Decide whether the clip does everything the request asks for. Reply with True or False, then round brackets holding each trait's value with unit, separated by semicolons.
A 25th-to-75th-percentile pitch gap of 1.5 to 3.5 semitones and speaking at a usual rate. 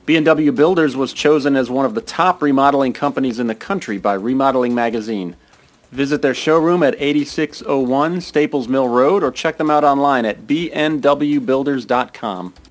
True (2.9 semitones; 150 wpm)